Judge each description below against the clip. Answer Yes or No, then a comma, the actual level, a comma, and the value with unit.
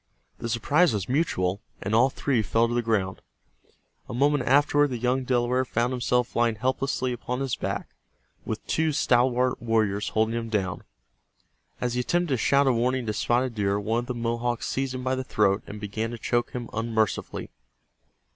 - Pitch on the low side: Yes, low, 120 Hz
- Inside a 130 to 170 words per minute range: No, average, 185 wpm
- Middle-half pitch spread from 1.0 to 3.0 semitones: Yes, narrow, 2.6 semitones